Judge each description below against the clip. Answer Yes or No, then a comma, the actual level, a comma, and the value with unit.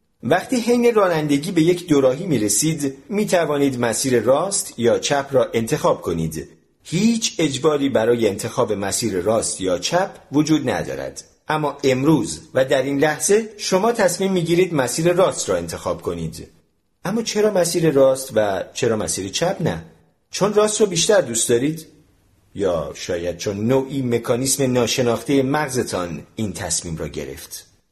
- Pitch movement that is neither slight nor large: No, wide, 7.4 semitones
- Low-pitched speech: No, medium, 145 Hz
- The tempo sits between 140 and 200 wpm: Yes, average, 145 wpm